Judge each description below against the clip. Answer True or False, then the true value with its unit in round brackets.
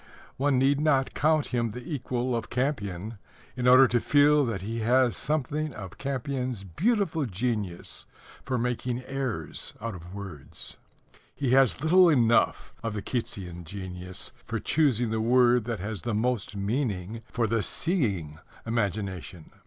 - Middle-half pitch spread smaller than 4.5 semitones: False (4.8 semitones)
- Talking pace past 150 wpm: False (145 wpm)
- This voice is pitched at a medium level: False (120 Hz)